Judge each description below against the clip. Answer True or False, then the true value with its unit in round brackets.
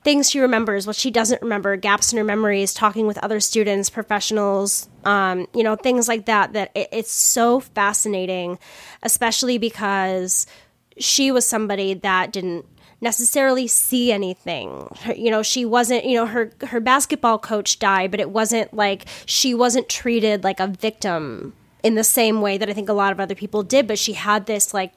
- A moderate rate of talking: True (185 wpm)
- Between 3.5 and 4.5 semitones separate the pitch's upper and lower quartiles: False (2.9 semitones)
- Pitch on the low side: False (215 Hz)